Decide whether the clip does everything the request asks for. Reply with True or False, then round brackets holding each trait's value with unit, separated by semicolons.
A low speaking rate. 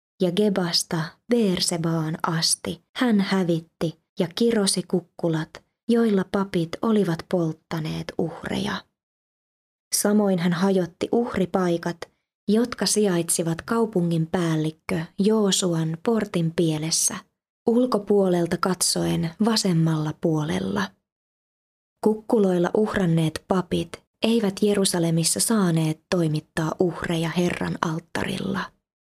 True (80 wpm)